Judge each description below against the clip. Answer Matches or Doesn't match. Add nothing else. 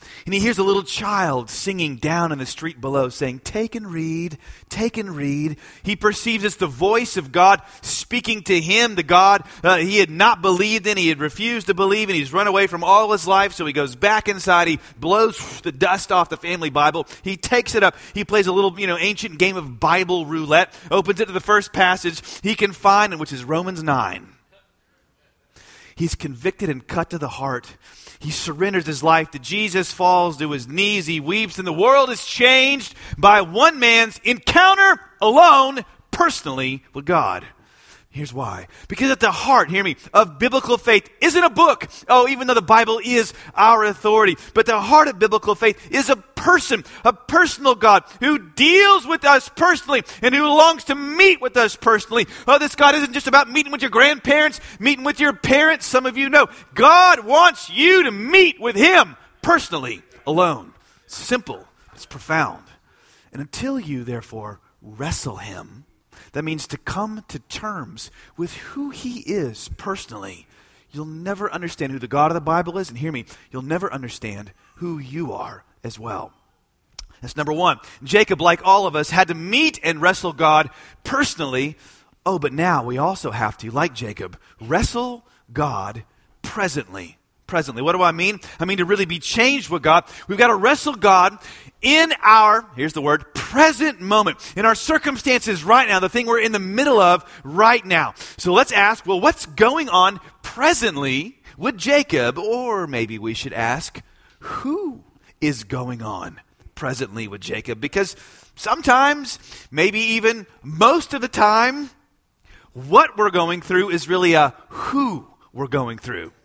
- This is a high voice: Matches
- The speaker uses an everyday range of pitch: Doesn't match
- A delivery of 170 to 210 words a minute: Matches